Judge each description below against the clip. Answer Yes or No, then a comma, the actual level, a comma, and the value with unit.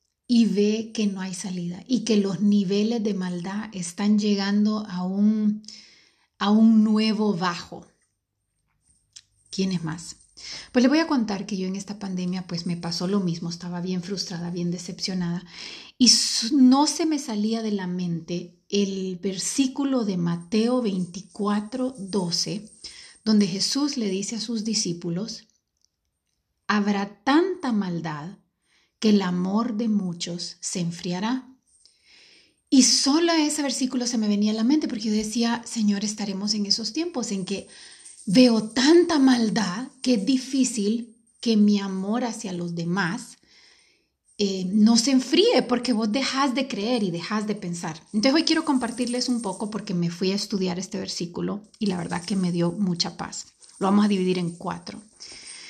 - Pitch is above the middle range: Yes, high, 210 Hz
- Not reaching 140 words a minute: No, average, 155 wpm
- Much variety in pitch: No, average, 4.1 semitones